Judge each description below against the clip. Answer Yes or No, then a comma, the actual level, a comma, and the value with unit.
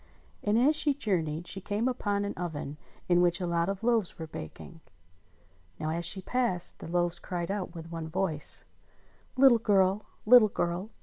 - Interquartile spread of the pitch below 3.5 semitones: No, average, 3.9 semitones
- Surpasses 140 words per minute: Yes, average, 180 wpm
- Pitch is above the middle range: No, medium, 180 Hz